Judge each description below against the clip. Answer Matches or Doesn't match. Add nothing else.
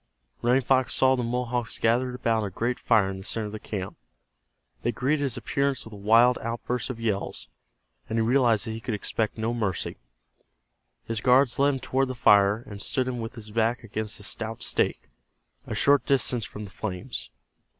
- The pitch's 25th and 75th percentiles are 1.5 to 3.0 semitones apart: Matches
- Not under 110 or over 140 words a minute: Doesn't match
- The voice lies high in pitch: Doesn't match